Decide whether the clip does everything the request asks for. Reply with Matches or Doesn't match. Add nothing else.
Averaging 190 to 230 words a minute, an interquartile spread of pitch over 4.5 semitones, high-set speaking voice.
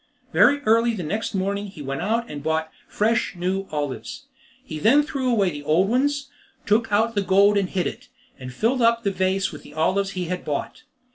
Matches